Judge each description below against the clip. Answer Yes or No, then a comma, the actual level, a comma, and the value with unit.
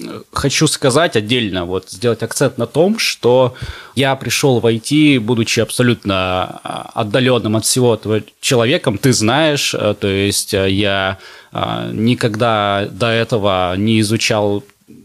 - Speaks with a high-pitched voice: No, low, 115 Hz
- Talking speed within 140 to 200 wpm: No, average, 120 wpm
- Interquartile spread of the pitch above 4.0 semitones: No, average, 3.6 semitones